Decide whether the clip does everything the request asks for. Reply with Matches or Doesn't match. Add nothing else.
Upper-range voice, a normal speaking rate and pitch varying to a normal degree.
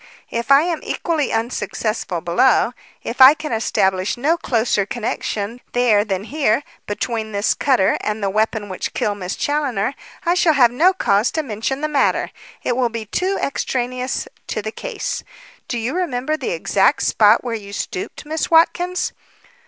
Doesn't match